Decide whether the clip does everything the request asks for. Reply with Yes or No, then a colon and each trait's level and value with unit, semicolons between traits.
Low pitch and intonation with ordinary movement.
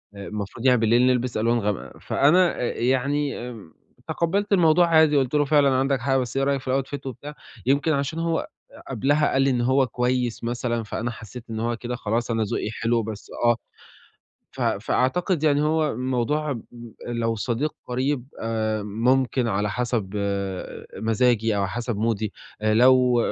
Yes: low, 125 Hz; average, 3.5 semitones